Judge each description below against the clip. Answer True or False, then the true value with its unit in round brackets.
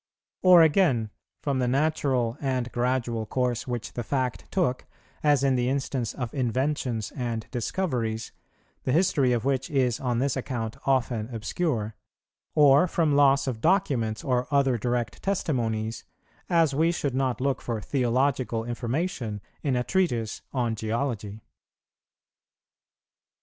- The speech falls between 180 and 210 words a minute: False (135 wpm)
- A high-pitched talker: False (125 Hz)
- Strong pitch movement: False (3.3 semitones)